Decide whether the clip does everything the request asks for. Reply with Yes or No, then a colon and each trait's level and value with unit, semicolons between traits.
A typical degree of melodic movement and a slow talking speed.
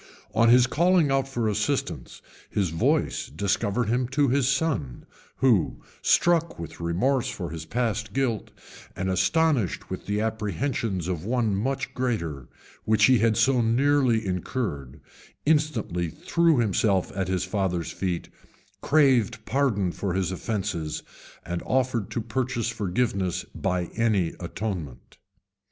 No: wide, 5.7 semitones; slow, 130 wpm